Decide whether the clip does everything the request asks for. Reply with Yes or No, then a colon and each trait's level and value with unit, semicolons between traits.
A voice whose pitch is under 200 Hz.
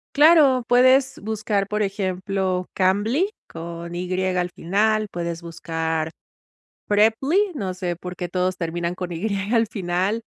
Yes: medium, 185 Hz